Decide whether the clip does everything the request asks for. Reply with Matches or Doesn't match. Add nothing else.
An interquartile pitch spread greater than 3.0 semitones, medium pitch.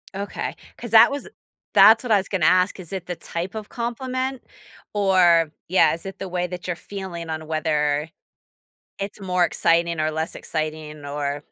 Matches